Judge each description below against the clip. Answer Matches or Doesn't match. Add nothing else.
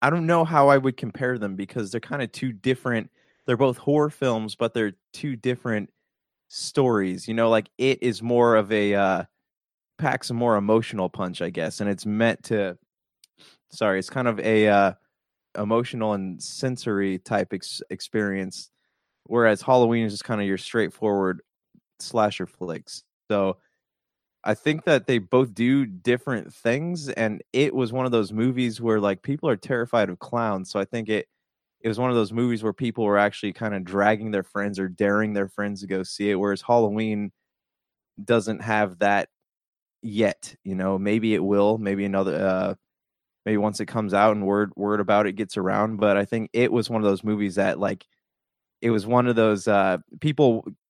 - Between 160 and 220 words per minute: Matches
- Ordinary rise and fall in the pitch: Matches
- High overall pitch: Doesn't match